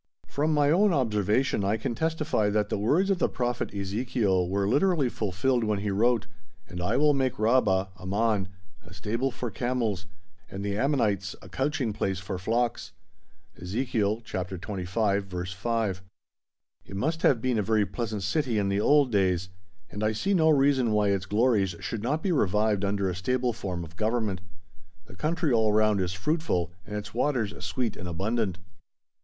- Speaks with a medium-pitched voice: No, low, 110 Hz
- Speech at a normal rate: Yes, average, 175 wpm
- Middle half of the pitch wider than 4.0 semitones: Yes, average, 4.6 semitones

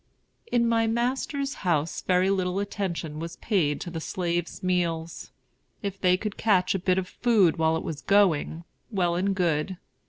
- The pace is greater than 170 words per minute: No, average, 165 wpm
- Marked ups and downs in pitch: No, average, 3.2 semitones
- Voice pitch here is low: No, medium, 185 Hz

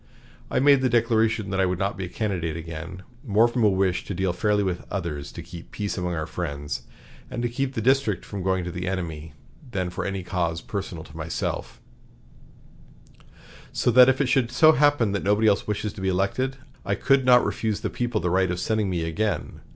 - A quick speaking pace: Yes, fast, 215 wpm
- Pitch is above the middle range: No, low, 100 Hz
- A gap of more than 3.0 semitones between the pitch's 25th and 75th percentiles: Yes, average, 4.7 semitones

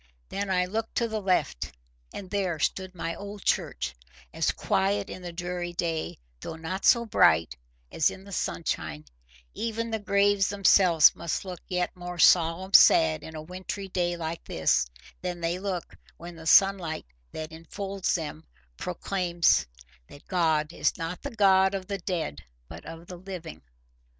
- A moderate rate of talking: Yes, average, 160 wpm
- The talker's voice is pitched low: No, medium, 180 Hz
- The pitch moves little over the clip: No, average, 3.1 semitones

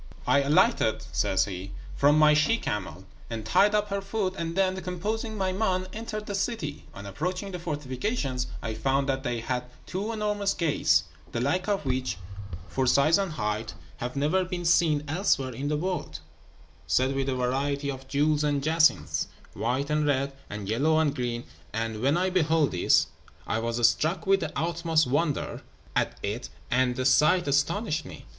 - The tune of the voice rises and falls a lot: Yes, wide, 6.1 semitones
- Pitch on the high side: No, medium, 150 Hz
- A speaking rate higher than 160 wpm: Yes, average, 175 wpm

